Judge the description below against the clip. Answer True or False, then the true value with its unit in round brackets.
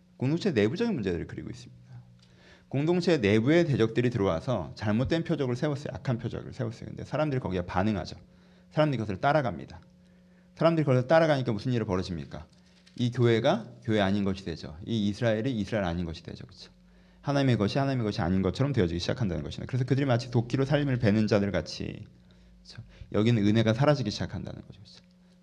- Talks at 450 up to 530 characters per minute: True (465 characters per minute)